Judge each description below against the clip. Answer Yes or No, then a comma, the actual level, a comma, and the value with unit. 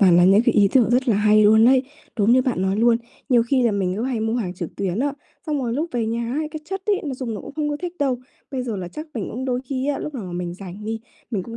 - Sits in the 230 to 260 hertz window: Yes, high, 235 Hz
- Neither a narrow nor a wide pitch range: Yes, average, 4.4 semitones